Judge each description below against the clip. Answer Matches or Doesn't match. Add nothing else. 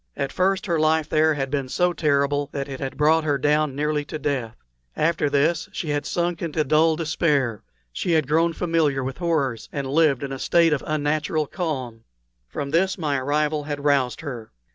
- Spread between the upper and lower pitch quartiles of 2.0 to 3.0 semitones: Matches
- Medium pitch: Matches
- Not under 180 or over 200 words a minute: Matches